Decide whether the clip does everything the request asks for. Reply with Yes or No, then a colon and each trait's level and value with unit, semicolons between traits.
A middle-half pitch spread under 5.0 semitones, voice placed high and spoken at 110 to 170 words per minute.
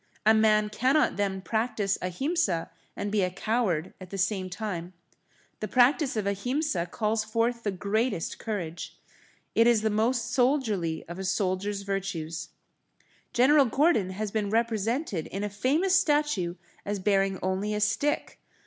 Yes: average, 3.8 semitones; high, 210 Hz; average, 150 wpm